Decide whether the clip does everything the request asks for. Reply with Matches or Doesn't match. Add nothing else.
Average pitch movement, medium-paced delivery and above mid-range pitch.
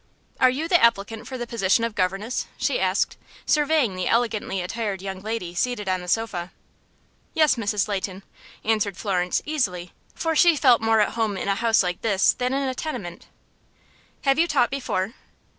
Matches